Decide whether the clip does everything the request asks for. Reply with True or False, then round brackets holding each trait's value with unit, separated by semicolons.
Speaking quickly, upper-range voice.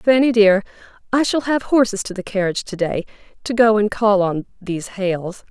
False (195 wpm; 210 Hz)